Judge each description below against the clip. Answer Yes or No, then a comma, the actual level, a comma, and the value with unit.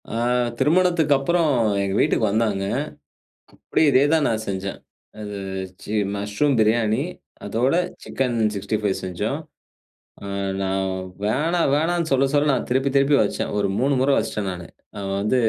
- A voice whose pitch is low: Yes, low, 120 Hz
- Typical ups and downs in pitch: No, wide, 5.9 semitones